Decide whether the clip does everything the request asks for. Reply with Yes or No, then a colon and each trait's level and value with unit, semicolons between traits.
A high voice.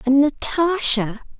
Yes: very high, 275 Hz